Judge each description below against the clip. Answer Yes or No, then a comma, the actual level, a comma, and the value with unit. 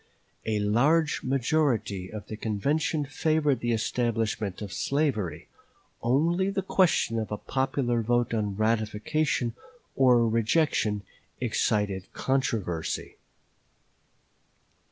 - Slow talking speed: Yes, slow, 95 wpm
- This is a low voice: Yes, low, 120 Hz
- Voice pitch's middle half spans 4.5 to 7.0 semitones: Yes, average, 5.0 semitones